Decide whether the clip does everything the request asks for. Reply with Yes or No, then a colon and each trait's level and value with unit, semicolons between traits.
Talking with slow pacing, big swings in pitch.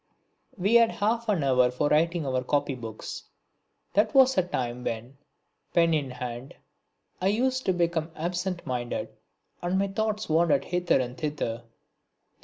No: average, 145 wpm; wide, 7.0 semitones